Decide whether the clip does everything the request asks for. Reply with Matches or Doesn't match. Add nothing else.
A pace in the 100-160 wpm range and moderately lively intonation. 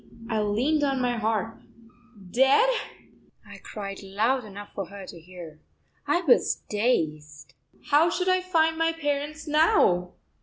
Doesn't match